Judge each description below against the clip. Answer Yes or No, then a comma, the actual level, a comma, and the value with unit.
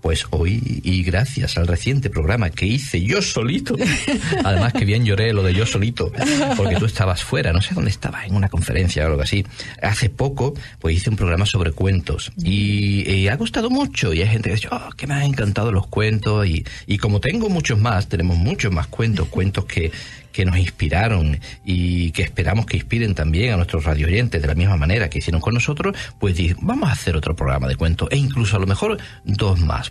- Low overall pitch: Yes, low, 100 Hz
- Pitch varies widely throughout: No, average, 4.7 semitones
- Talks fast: Yes, fast, 215 wpm